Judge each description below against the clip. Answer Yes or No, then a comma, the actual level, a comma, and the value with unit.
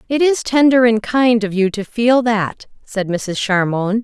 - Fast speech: No, average, 195 wpm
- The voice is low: No, high, 225 Hz